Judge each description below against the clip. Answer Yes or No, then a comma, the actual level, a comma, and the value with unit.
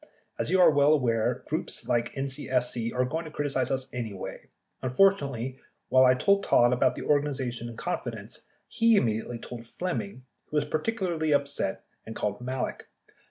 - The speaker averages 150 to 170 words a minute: Yes, average, 160 wpm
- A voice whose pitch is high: No, low, 130 Hz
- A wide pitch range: No, average, 3.8 semitones